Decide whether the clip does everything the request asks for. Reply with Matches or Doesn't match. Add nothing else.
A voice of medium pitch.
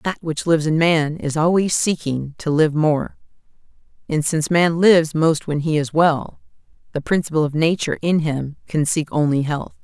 Matches